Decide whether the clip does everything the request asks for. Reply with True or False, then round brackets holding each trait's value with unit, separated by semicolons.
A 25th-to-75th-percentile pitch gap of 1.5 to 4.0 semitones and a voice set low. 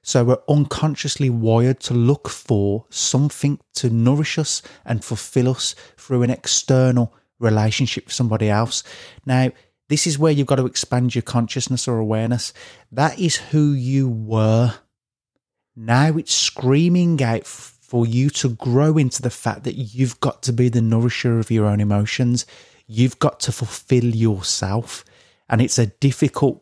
True (3.2 semitones; 125 Hz)